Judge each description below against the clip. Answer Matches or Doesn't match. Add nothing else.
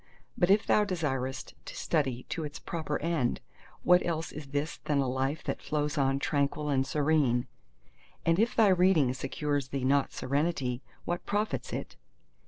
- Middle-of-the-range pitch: Matches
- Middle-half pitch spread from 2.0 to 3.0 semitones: Doesn't match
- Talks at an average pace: Matches